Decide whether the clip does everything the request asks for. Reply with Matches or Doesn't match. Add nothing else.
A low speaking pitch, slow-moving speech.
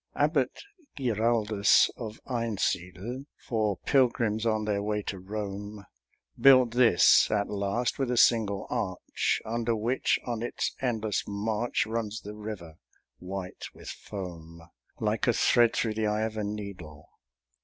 Matches